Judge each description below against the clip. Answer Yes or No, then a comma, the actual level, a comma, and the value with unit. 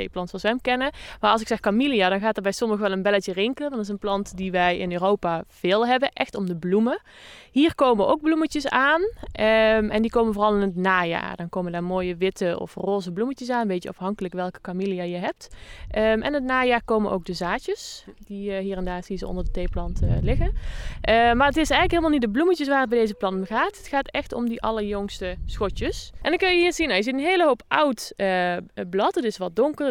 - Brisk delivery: Yes, fast, 250 wpm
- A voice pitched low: No, high, 215 Hz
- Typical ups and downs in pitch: No, wide, 5.9 semitones